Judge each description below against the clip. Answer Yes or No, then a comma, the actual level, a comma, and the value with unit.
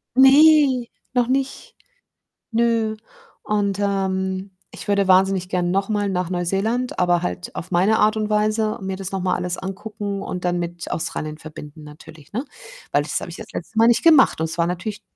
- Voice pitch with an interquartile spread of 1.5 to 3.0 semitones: No, average, 3.7 semitones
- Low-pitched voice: No, high, 195 Hz